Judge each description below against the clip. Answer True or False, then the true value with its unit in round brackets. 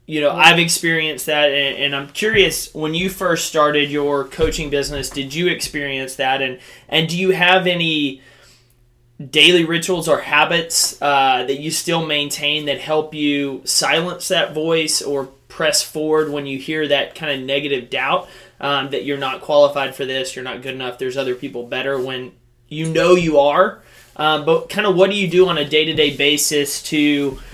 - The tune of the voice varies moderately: True (3.0 semitones)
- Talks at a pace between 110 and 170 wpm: False (190 wpm)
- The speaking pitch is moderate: True (145 Hz)